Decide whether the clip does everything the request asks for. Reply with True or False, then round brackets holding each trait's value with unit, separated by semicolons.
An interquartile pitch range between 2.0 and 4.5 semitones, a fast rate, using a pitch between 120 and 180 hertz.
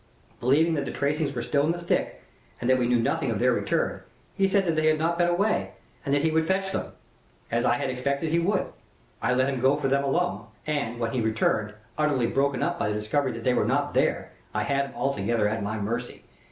False (4.9 semitones; 240 wpm; 140 Hz)